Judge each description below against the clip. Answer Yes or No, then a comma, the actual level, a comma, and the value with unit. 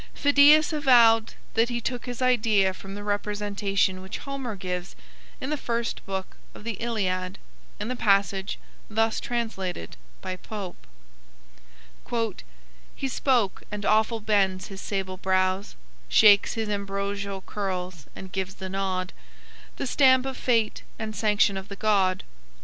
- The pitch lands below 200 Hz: No, high, 205 Hz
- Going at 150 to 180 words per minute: No, average, 140 wpm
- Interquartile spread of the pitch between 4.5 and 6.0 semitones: No, average, 3.4 semitones